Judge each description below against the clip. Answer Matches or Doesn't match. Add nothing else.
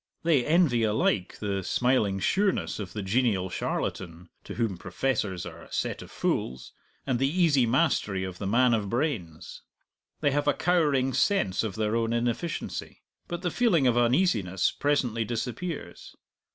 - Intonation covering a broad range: Matches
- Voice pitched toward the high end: Doesn't match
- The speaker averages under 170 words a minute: Matches